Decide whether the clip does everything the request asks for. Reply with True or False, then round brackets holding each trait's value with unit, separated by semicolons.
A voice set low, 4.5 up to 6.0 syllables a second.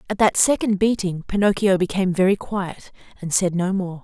False (190 Hz; 5.4 syllables/s)